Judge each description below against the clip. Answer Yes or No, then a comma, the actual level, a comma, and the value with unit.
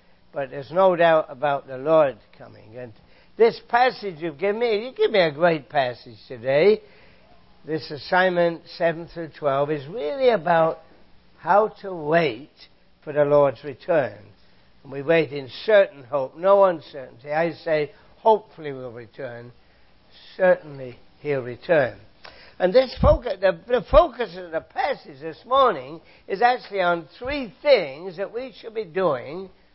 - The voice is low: No, medium, 165 Hz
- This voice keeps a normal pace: Yes, average, 145 wpm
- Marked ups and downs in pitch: Yes, wide, 5.9 semitones